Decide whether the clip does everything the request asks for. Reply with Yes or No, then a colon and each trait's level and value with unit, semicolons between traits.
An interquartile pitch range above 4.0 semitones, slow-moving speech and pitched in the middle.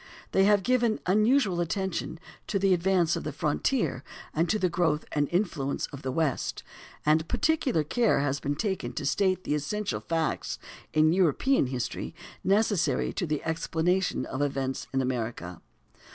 No: average, 5.2 semitones; average, 155 wpm; medium, 165 Hz